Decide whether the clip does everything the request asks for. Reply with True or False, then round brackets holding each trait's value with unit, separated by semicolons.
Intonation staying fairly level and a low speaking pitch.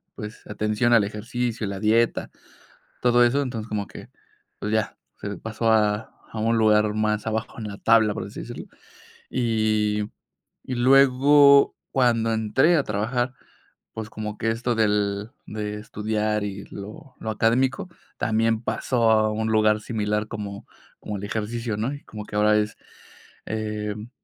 True (1.9 semitones; 110 Hz)